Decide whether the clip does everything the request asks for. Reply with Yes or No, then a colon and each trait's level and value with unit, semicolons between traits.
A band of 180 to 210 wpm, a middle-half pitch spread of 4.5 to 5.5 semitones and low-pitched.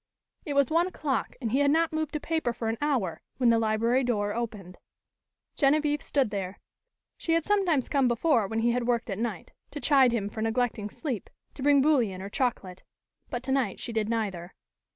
No: average, 195 wpm; average, 4.8 semitones; high, 245 Hz